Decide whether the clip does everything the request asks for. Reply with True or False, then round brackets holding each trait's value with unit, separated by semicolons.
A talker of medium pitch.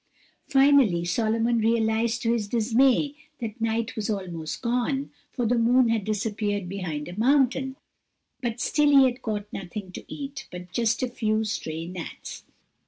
False (225 Hz)